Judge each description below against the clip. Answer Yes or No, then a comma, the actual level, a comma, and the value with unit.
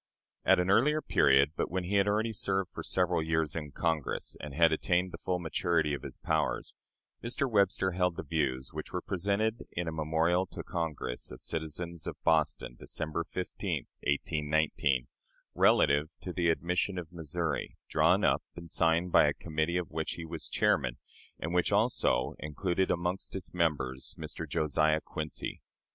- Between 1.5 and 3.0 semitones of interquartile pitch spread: Yes, average, 2.7 semitones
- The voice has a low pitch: Yes, very low, 85 Hz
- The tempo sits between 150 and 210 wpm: Yes, average, 165 wpm